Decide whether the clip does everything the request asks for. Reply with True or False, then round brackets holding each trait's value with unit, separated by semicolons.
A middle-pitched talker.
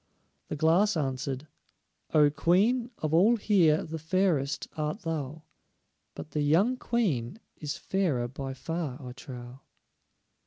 True (155 Hz)